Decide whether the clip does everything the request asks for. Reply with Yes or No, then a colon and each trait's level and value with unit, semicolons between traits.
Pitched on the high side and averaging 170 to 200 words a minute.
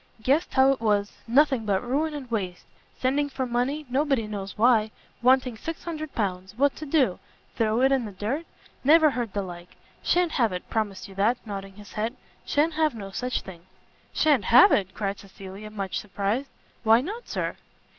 Yes: high, 230 Hz; average, 180 wpm